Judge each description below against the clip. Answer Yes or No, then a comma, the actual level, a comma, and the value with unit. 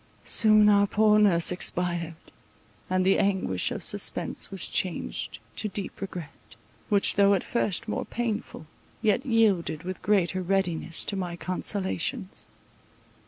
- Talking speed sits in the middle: No, slow, 130 wpm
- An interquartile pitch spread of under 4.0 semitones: Yes, average, 3.0 semitones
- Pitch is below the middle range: No, high, 195 Hz